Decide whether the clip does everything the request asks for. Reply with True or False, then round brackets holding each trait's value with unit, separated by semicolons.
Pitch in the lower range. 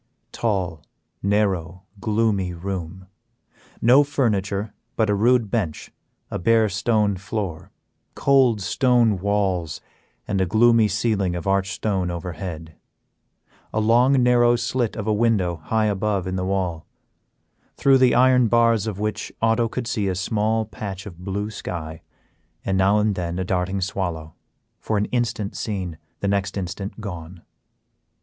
True (100 Hz)